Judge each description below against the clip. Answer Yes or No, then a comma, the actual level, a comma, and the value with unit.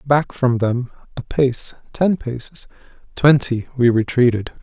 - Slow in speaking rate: Yes, slow, 130 wpm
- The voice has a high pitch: No, low, 125 Hz